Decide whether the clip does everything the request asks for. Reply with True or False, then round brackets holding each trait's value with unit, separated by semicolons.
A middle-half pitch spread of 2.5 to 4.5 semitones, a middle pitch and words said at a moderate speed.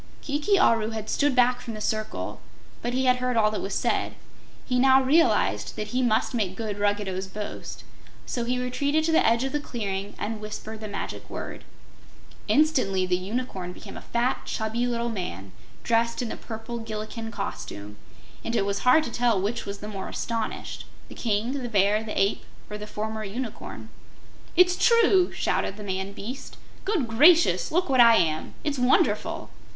False (3.5 semitones; 230 Hz; 180 wpm)